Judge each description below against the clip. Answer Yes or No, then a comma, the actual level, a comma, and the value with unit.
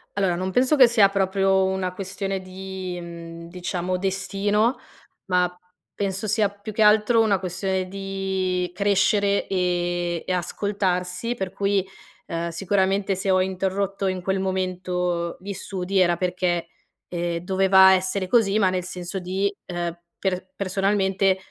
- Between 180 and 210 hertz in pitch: Yes, high, 190 Hz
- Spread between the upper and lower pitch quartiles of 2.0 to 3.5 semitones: No, narrow, 1.5 semitones